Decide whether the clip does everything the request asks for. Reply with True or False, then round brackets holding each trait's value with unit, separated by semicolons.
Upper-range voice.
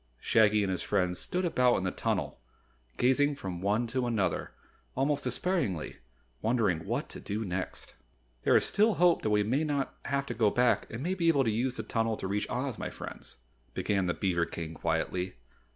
False (115 Hz)